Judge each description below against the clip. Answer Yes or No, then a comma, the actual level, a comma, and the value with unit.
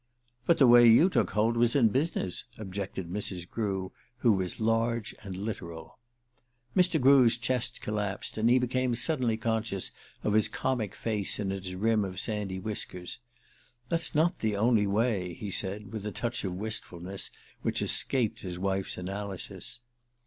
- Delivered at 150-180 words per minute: Yes, average, 155 wpm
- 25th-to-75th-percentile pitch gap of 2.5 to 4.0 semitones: Yes, average, 3.7 semitones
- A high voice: No, low, 110 Hz